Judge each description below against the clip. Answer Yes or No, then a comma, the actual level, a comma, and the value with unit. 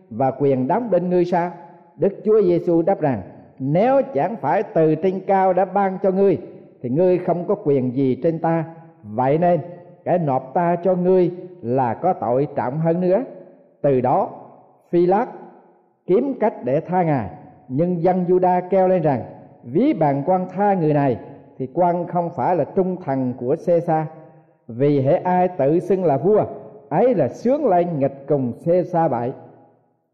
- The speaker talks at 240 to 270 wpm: No, average, 175 wpm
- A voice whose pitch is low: No, medium, 170 Hz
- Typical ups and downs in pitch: Yes, average, 4.5 semitones